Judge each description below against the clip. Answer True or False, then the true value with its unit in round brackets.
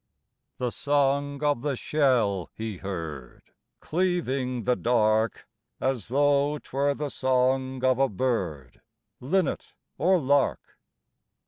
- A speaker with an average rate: False (110 wpm)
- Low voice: True (130 Hz)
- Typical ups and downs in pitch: True (4.1 semitones)